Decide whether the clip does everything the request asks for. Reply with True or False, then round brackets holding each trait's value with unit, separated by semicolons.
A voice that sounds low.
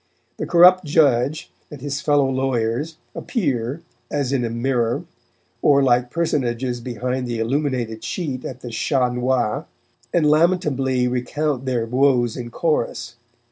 True (130 Hz)